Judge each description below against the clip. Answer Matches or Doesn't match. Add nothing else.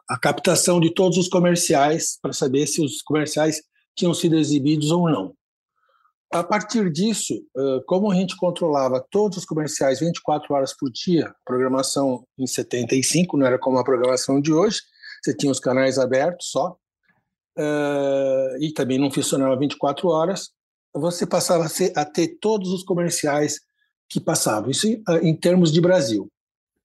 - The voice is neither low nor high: Matches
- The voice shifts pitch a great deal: Doesn't match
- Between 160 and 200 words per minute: Doesn't match